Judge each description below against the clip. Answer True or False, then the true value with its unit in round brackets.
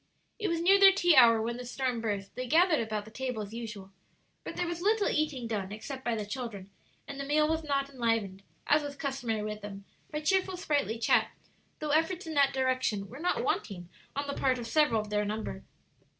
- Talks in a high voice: True (255 Hz)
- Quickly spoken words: True (215 wpm)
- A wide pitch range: True (5.9 semitones)